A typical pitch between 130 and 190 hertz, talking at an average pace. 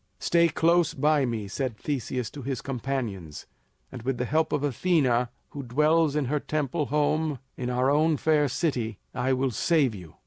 Yes: low, 135 Hz; average, 175 wpm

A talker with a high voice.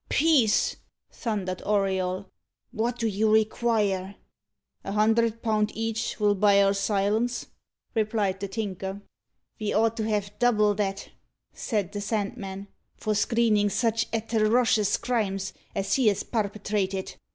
Yes: high, 210 Hz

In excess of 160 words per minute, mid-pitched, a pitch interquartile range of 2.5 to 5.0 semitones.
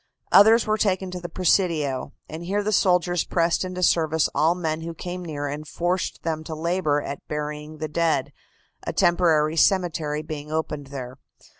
Yes: average, 170 wpm; medium, 165 Hz; average, 2.9 semitones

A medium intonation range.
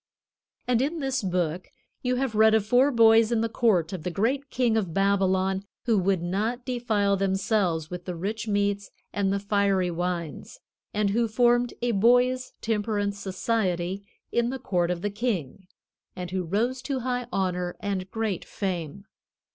Yes: average, 4.1 semitones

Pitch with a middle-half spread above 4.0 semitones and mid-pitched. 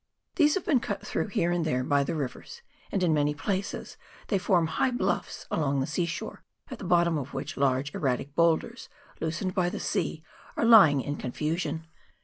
Yes: average, 4.8 semitones; medium, 165 Hz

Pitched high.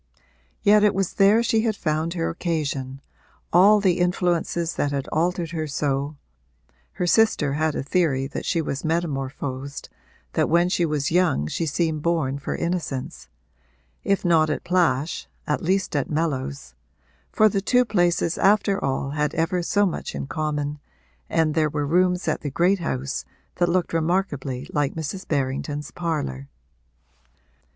No: medium, 160 Hz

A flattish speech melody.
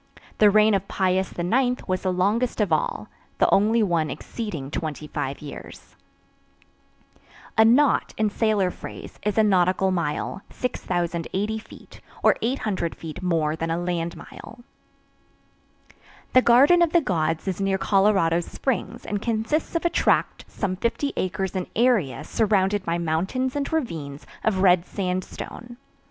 No: average, 4.5 semitones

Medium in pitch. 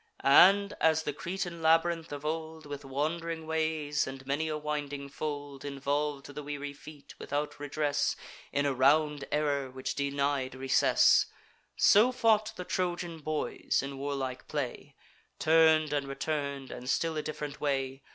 Yes: medium, 145 Hz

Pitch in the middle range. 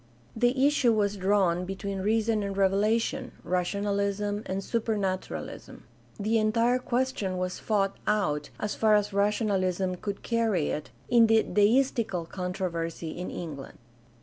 No: high, 205 Hz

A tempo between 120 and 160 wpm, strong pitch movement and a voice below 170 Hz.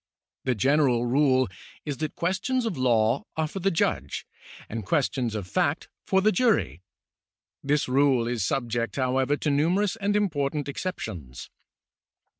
Yes: average, 140 wpm; wide, 5.9 semitones; medium, 140 Hz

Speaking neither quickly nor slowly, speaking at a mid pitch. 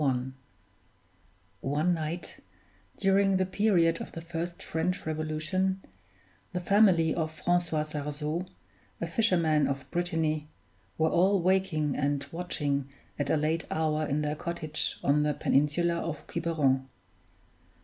No: slow, 120 wpm; medium, 160 Hz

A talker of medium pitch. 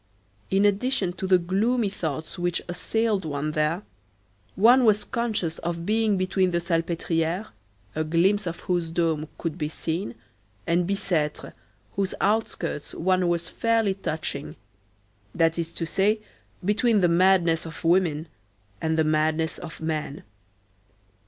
Yes: medium, 175 Hz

